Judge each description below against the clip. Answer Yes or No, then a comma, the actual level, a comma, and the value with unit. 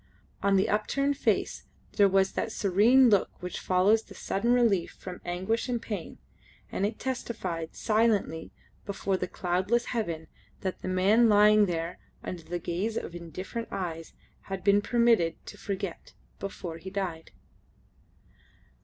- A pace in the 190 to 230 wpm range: No, average, 145 wpm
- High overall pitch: Yes, high, 195 Hz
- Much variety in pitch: No, average, 3.8 semitones